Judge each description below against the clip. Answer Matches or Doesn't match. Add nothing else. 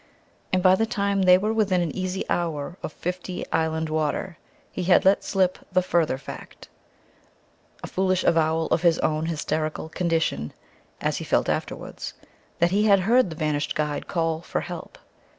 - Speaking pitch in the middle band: Matches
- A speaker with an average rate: Matches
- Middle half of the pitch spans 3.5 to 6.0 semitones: Doesn't match